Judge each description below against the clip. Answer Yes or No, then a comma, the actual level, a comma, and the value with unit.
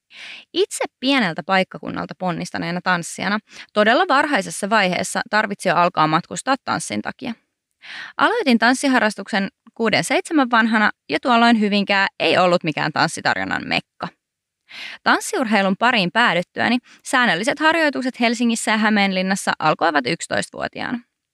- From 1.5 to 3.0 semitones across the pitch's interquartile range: No, average, 4.9 semitones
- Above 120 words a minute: No, average, 100 wpm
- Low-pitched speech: No, high, 215 Hz